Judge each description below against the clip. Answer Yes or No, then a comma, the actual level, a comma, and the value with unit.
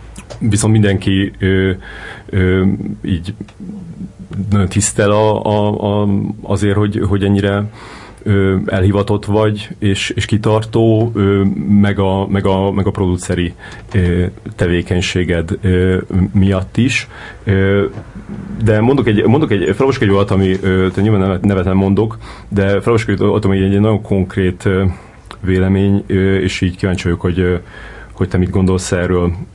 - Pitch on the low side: Yes, low, 100 Hz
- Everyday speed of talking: Yes, average, 130 wpm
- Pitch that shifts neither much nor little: No, narrow, 1.8 semitones